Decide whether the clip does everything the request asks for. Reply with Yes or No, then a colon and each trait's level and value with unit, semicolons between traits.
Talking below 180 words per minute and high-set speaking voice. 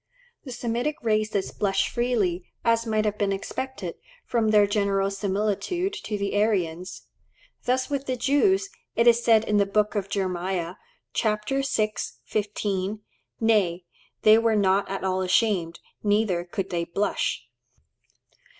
Yes: average, 140 wpm; high, 210 Hz